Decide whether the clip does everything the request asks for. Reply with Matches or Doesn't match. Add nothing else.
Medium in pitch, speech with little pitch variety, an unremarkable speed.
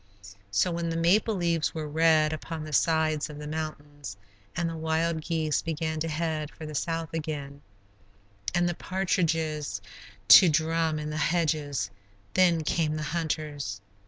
Matches